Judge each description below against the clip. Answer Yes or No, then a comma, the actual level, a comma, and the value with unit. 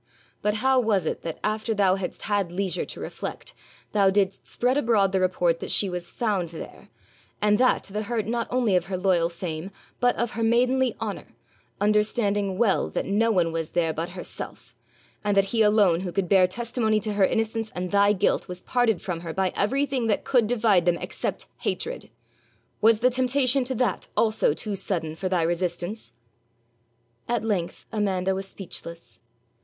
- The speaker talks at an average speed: Yes, average, 180 wpm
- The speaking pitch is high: Yes, high, 200 Hz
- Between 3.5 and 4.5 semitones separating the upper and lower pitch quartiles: Yes, average, 3.9 semitones